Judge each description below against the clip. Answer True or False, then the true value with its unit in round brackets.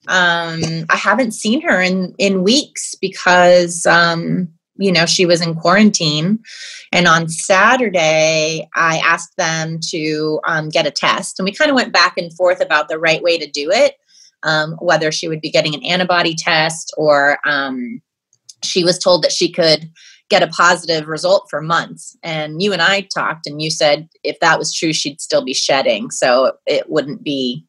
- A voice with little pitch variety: False (3.7 semitones)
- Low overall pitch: False (175 Hz)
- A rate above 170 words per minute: True (185 wpm)